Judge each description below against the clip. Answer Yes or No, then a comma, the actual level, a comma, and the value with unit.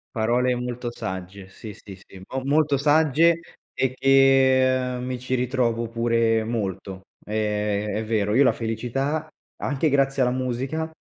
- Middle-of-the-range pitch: No, low, 125 Hz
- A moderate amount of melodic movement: Yes, average, 3.5 semitones